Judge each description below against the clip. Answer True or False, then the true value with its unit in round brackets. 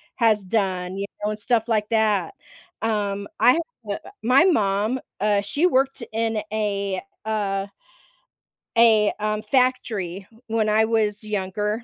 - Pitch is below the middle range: False (215 Hz)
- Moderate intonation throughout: False (2.1 semitones)